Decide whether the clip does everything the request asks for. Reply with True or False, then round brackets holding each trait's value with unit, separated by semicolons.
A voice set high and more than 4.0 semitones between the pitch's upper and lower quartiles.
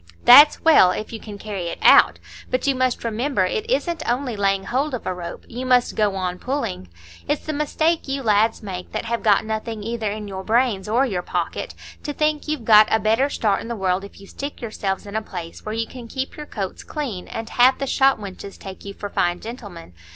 True (220 Hz; 4.8 semitones)